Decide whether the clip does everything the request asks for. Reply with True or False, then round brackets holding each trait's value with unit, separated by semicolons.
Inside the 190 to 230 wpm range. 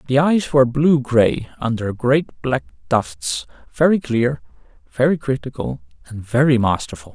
False (135 wpm)